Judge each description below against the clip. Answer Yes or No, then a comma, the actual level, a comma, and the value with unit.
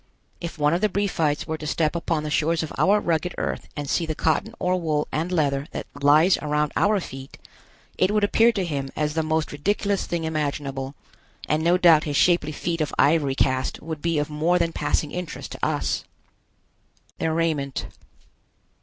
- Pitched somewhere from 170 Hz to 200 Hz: No, medium, 160 Hz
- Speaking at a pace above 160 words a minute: Yes, average, 190 wpm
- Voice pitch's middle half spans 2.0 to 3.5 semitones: Yes, average, 2.8 semitones